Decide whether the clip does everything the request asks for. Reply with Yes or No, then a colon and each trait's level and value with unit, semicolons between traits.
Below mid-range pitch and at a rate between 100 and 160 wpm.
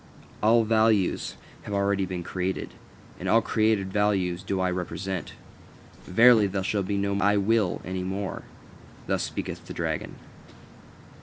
Yes: low, 100 Hz; average, 140 wpm